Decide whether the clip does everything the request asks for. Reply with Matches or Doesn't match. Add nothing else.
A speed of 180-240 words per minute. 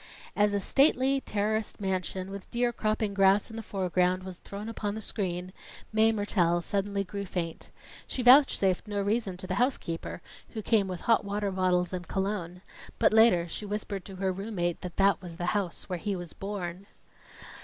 Matches